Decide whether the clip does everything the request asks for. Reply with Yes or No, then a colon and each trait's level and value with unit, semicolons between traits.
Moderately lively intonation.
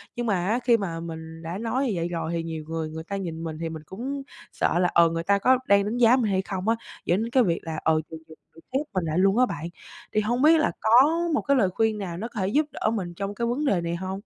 No: wide, 5.7 semitones